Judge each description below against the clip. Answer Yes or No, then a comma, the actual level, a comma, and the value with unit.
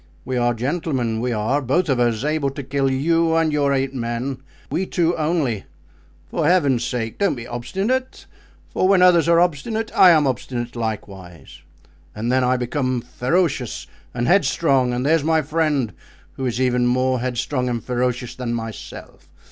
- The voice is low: Yes, low, 130 Hz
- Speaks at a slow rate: No, average, 165 wpm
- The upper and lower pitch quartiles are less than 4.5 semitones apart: No, average, 4.8 semitones